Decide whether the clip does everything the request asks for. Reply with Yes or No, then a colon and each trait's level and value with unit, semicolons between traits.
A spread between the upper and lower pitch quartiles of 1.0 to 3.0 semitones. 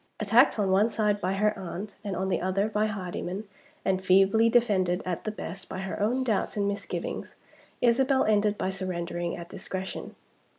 Yes: narrow, 2.4 semitones